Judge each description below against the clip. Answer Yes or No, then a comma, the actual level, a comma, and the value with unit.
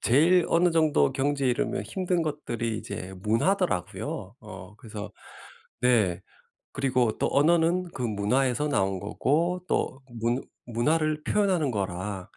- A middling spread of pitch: No, wide, 7.4 semitones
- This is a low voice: Yes, low, 130 Hz